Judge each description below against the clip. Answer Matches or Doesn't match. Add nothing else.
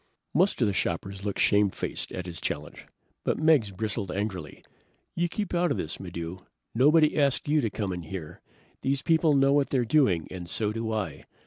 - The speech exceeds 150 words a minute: Matches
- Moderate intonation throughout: Doesn't match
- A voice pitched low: Matches